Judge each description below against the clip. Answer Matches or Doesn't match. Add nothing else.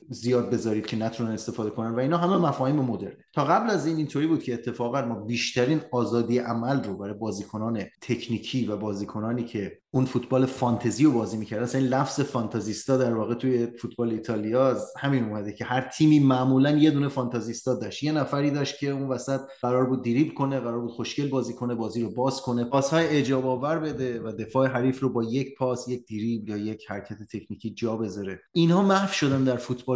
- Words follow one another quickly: Matches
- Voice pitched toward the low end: Matches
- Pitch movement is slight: Doesn't match